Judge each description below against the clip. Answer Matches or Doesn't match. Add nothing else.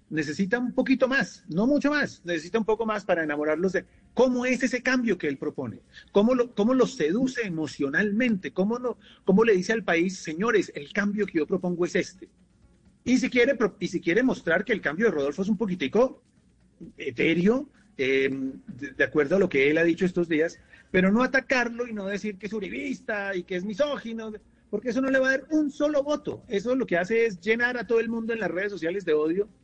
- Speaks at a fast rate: Matches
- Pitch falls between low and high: Doesn't match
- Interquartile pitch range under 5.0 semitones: Doesn't match